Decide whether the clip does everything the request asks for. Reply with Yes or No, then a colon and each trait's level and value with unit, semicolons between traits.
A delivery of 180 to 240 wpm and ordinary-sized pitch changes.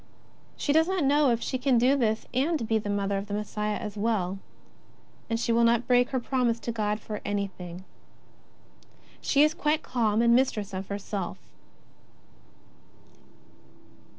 No: average, 155 wpm; average, 4.0 semitones